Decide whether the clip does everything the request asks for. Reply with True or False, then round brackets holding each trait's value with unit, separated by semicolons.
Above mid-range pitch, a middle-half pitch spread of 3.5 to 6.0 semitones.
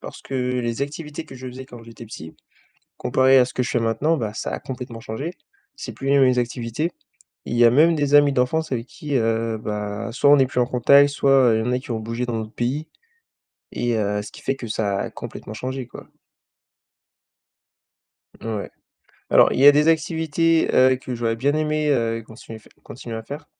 False (125 Hz; 3.8 semitones)